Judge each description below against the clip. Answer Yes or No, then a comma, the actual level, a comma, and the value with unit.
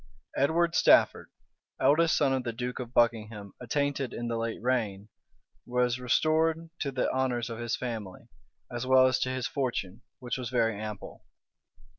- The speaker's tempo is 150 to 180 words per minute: Yes, average, 160 wpm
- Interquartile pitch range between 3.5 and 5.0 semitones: No, narrow, 2.4 semitones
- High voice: No, low, 125 Hz